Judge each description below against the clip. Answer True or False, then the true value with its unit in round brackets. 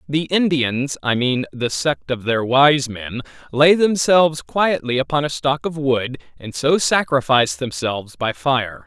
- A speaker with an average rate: True (160 wpm)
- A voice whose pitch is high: False (135 Hz)